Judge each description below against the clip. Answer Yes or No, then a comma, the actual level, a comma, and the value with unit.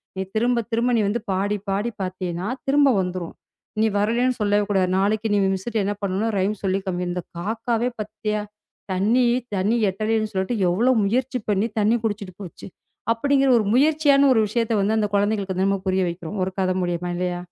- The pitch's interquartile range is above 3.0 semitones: Yes, average, 3.5 semitones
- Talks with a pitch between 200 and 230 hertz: Yes, high, 205 Hz